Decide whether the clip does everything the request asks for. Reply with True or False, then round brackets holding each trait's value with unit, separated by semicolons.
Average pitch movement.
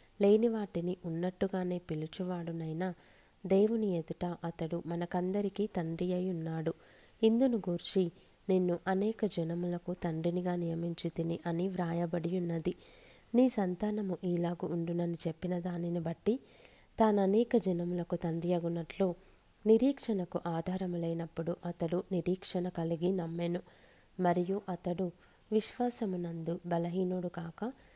False (2.1 semitones)